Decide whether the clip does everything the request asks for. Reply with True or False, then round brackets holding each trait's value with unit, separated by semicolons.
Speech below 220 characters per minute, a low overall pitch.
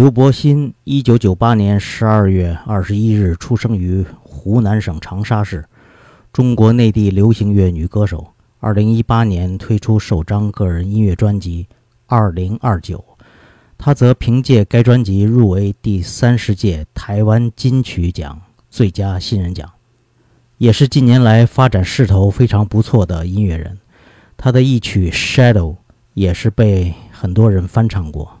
False (235 characters per minute; 105 Hz)